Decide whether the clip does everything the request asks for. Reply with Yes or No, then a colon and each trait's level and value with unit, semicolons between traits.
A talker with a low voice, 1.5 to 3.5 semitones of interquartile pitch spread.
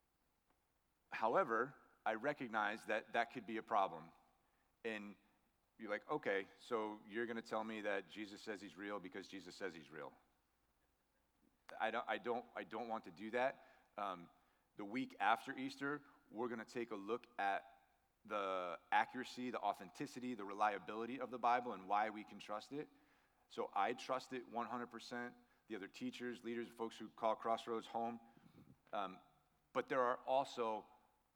Yes: low, 115 Hz; average, 2.9 semitones